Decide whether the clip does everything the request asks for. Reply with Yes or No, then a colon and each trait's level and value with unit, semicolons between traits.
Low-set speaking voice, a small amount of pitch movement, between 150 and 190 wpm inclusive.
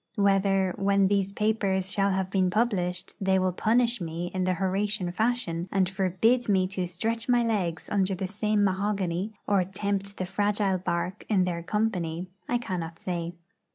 No: high, 195 Hz; narrow, 2.2 semitones; average, 165 wpm